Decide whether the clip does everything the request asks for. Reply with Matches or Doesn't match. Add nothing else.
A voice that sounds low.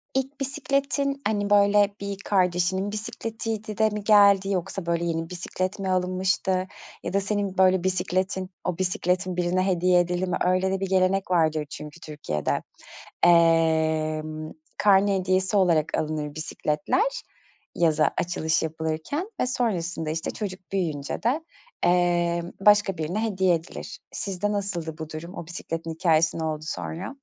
Doesn't match